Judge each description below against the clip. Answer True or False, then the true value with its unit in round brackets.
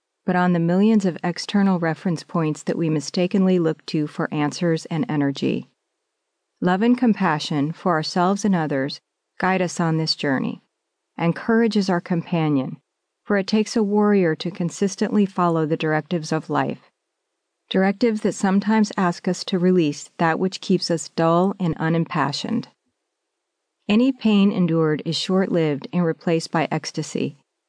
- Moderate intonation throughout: True (3.3 semitones)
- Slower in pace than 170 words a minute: True (150 wpm)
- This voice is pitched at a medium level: True (175 Hz)